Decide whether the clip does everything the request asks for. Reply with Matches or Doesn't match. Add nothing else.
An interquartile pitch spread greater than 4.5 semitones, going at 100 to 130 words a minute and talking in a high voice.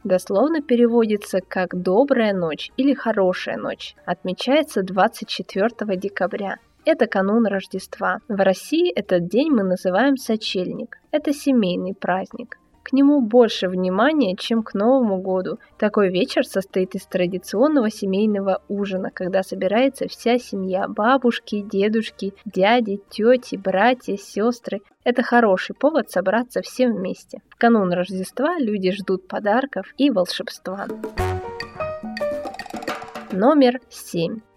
Matches